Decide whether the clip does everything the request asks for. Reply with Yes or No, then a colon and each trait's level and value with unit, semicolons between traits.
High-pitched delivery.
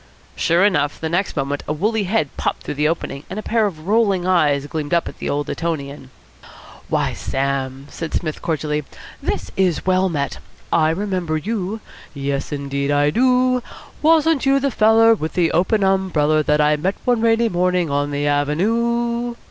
No: medium, 170 Hz